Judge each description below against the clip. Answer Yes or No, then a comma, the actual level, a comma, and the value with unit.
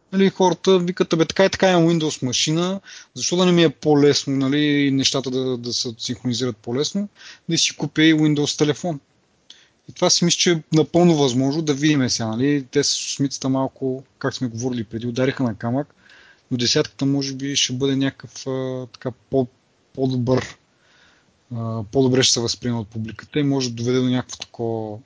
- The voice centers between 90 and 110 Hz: No, low, 135 Hz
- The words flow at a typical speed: No, fast, 180 wpm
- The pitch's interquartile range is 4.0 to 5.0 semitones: No, average, 3.6 semitones